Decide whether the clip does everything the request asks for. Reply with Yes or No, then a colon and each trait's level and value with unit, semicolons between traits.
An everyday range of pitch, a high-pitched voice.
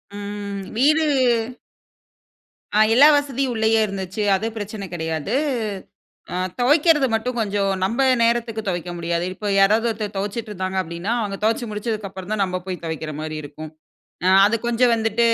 Yes: average, 3.6 semitones; high, 210 Hz